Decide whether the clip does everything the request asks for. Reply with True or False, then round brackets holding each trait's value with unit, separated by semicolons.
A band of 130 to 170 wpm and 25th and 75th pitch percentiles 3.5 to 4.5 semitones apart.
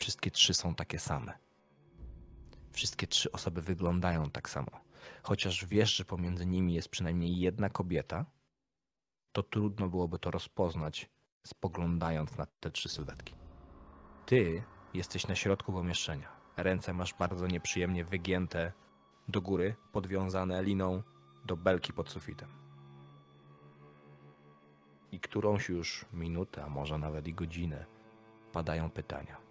False (120 wpm; 4.2 semitones)